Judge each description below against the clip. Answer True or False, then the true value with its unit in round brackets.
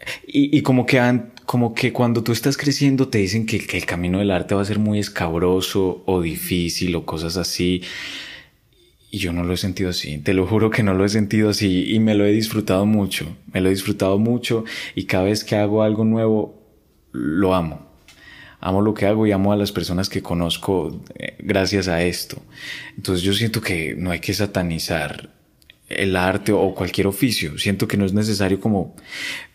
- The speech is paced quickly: True (200 wpm)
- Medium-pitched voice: False (100 Hz)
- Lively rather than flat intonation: False (2.9 semitones)